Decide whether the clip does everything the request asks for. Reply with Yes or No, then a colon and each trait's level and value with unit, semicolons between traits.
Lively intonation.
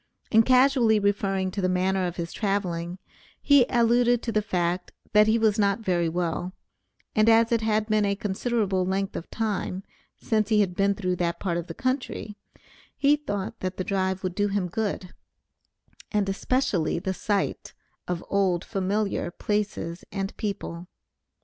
No: average, 3.0 semitones